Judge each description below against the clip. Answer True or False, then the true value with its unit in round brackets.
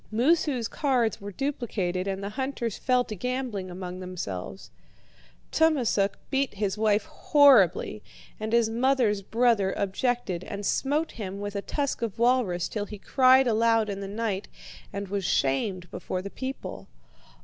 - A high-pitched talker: True (215 Hz)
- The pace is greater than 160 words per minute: False (150 wpm)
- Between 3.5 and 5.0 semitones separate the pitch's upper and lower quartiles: True (4.6 semitones)